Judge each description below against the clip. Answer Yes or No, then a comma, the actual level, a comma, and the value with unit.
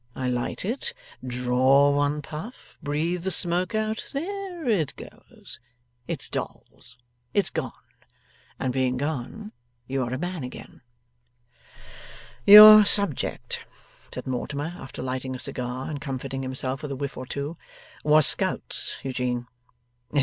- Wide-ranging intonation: Yes, wide, 5.8 semitones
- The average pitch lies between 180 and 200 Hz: No, medium, 145 Hz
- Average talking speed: No, slow, 130 wpm